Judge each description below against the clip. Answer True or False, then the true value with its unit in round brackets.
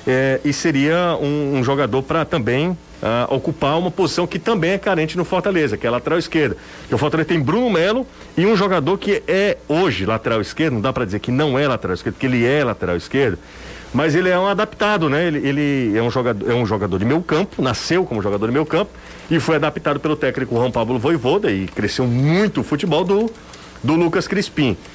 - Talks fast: True (220 wpm)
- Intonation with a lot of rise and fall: True (5.7 semitones)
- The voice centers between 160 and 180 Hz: False (150 Hz)